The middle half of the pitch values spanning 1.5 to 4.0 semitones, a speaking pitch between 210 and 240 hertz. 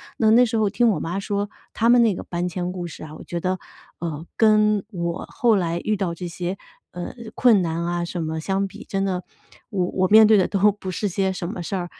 No: average, 3.4 semitones; high, 190 Hz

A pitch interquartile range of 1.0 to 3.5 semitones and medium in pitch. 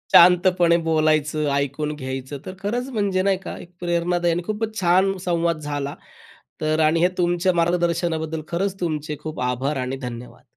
Yes: average, 2.9 semitones; medium, 170 Hz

